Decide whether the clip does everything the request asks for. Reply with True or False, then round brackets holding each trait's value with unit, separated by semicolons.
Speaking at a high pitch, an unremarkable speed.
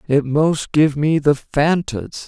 False (150 Hz; 185 wpm)